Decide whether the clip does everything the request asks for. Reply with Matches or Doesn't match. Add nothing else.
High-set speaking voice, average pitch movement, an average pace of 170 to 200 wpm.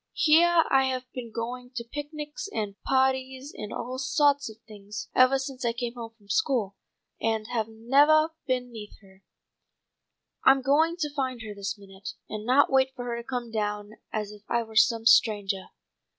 Matches